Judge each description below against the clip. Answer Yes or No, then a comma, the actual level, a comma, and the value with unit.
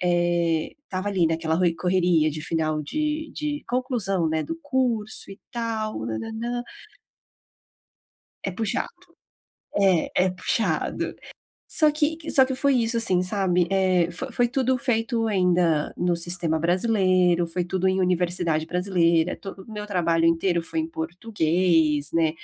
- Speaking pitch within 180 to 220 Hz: Yes, medium, 185 Hz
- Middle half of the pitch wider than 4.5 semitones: Yes, average, 5.1 semitones